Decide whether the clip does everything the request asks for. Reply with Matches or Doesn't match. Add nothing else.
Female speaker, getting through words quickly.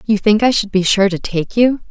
Matches